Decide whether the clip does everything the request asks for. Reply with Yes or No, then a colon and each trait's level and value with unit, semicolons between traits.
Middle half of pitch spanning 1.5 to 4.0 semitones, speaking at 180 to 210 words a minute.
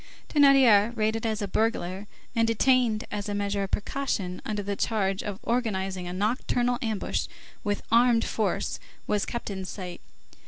No: average, 2.9 semitones; average, 155 wpm